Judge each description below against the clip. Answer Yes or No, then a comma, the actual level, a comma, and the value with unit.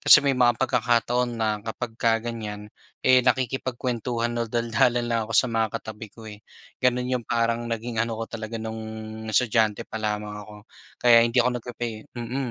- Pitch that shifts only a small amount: Yes, narrow, 1.7 semitones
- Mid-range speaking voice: No, low, 115 Hz